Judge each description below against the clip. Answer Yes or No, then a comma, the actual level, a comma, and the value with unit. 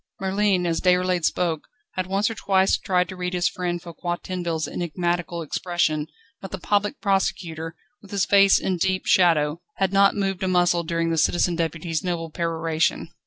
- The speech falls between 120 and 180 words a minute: Yes, average, 170 wpm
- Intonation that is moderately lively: No, narrow, 2.3 semitones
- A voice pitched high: No, medium, 180 Hz